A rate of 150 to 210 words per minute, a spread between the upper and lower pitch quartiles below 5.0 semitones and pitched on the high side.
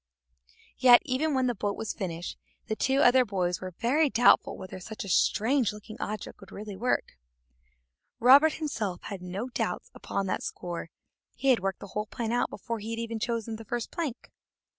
Yes: average, 185 wpm; average, 4.2 semitones; high, 225 Hz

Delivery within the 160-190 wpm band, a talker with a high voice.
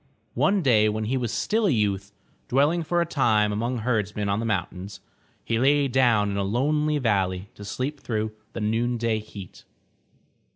No: average, 170 wpm; low, 115 Hz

